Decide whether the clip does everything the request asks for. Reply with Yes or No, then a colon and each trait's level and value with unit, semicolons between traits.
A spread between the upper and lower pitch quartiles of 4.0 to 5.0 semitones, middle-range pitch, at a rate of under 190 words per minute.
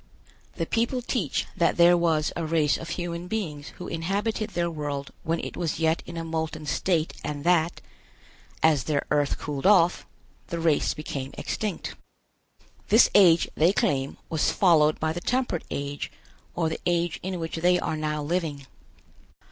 No: narrow, 2.5 semitones; medium, 165 Hz; average, 165 wpm